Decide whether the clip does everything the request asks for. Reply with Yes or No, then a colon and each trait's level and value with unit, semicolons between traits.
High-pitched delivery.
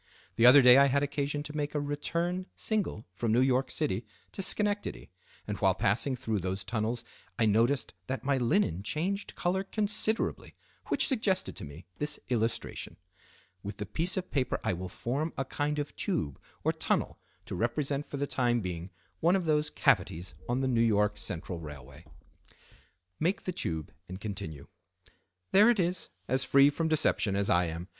No: low, 130 Hz